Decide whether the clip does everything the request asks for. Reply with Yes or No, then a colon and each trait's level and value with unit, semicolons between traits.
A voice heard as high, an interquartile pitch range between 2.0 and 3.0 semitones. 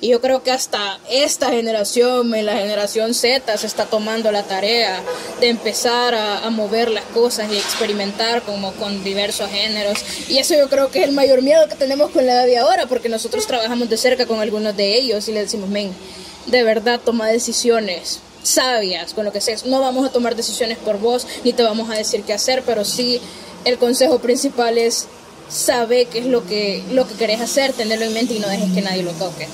Yes: high, 230 Hz; average, 2.7 semitones